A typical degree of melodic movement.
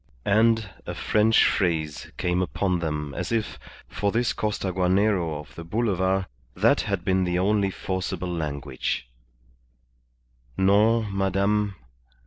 Yes: average, 3.1 semitones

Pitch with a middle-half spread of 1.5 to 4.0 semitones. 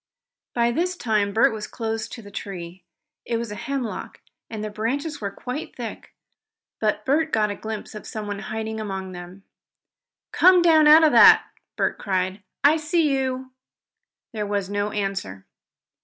No: average, 4.8 semitones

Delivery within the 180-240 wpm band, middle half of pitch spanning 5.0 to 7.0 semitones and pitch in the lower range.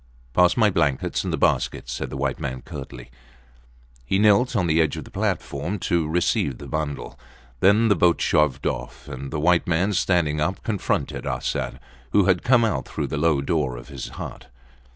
Yes: average, 190 wpm; wide, 5.4 semitones; very low, 80 Hz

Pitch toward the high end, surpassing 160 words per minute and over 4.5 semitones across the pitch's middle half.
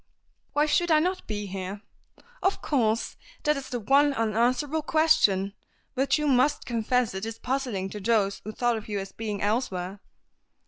Yes: high, 230 Hz; average, 170 wpm; wide, 5.5 semitones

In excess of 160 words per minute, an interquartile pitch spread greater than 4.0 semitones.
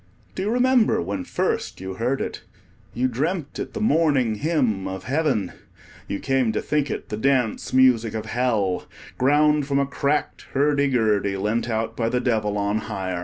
Yes: average, 175 wpm; average, 5.1 semitones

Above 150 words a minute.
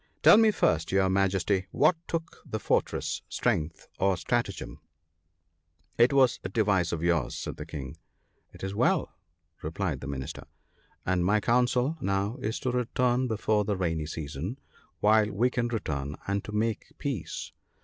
Yes: average, 160 wpm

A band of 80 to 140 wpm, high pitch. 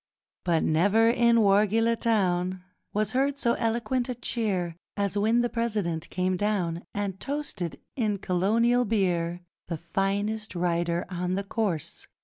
Yes: slow, 135 wpm; high, 205 Hz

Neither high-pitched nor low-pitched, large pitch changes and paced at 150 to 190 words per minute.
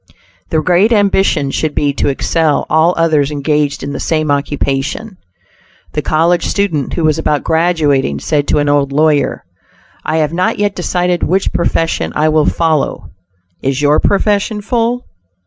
No: medium, 155 Hz; average, 3.6 semitones; average, 155 wpm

